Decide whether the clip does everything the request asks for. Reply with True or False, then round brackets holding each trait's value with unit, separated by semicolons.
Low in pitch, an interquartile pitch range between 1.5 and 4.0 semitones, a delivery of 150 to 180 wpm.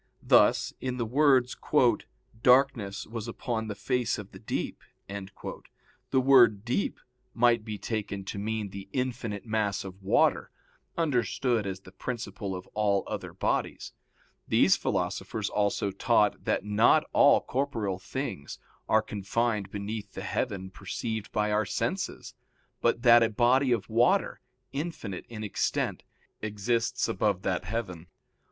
False (110 Hz; 3.3 semitones; 135 wpm)